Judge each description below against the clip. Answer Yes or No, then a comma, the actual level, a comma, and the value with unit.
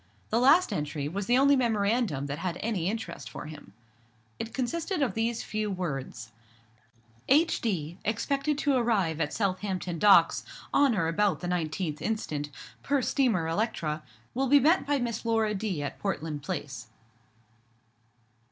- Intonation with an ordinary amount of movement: No, wide, 6.9 semitones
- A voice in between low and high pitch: No, high, 205 Hz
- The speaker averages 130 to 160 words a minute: Yes, average, 145 wpm